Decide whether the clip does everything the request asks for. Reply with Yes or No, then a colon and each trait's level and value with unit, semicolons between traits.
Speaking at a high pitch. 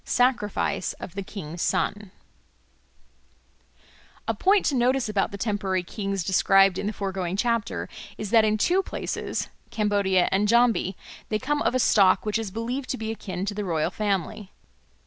Yes: high, 205 Hz